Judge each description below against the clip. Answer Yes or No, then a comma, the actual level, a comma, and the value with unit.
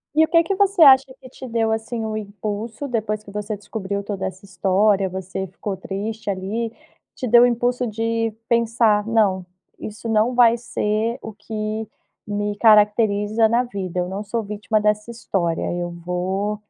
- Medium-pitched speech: No, high, 215 Hz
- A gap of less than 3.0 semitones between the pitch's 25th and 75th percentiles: Yes, narrow, 2.4 semitones